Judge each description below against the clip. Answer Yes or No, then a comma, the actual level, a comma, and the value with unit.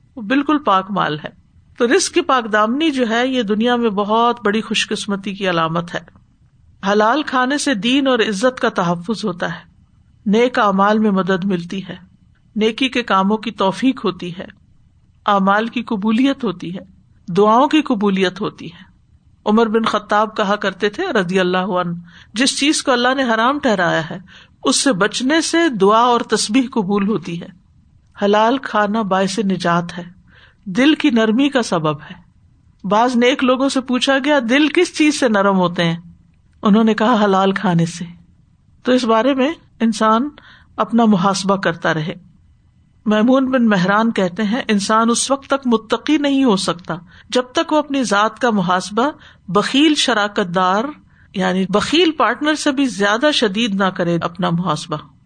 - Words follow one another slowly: No, average, 170 wpm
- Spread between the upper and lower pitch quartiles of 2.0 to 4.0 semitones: No, average, 4.9 semitones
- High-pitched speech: Yes, high, 215 Hz